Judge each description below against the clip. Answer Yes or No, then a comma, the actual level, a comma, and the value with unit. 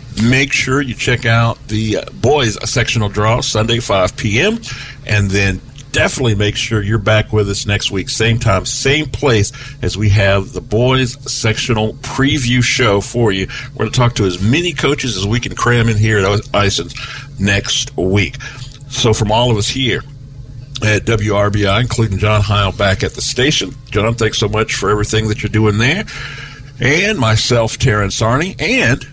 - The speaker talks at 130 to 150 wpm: No, average, 175 wpm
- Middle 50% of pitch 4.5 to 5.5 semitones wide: No, average, 3.8 semitones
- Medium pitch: No, low, 115 Hz